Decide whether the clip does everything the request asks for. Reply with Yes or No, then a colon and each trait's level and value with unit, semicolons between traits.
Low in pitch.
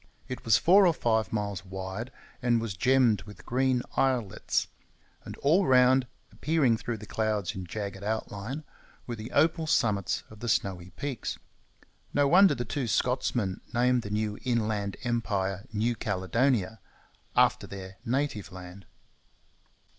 Yes: low, 110 Hz